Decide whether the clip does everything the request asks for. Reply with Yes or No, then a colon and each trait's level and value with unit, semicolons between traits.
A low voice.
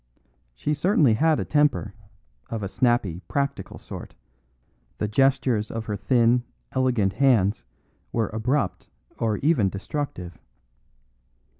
Yes: low, 120 Hz